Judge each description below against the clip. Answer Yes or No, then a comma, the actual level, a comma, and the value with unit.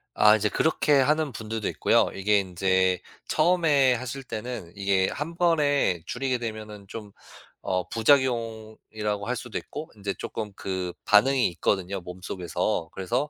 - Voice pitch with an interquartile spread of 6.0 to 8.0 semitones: No, average, 5.3 semitones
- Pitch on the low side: Yes, low, 110 Hz